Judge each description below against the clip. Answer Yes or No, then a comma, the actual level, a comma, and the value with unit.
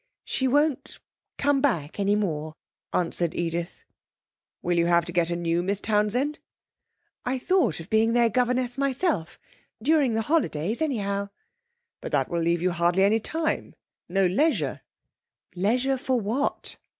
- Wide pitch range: Yes, wide, 7.2 semitones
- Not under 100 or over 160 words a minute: Yes, average, 145 wpm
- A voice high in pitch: Yes, high, 210 Hz